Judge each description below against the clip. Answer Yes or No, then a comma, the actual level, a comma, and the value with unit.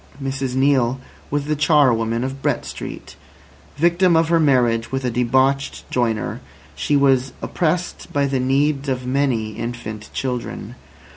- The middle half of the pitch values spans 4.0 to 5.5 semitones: No, average, 2.7 semitones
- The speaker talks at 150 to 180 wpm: No, average, 140 wpm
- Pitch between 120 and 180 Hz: Yes, low, 135 Hz